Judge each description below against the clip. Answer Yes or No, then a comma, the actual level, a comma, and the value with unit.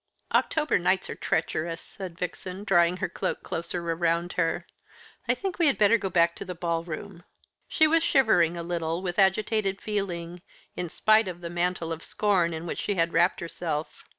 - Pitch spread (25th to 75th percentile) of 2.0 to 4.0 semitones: Yes, average, 2.9 semitones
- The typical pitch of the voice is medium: Yes, medium, 175 Hz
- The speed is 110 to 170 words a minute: No, average, 185 wpm